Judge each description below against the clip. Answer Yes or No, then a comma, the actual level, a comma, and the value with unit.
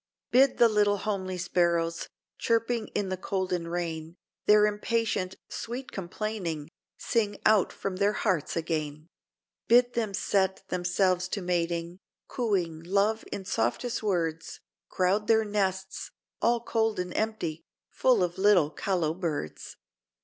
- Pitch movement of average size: Yes, average, 3.7 semitones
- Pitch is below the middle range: No, high, 190 Hz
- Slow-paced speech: Yes, slow, 130 wpm